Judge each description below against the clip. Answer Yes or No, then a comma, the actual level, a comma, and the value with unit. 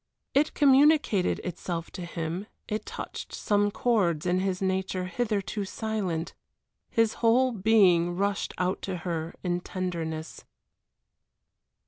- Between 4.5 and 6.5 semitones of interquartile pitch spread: No, average, 3.8 semitones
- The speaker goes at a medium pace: No, slow, 115 wpm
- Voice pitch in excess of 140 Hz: Yes, high, 190 Hz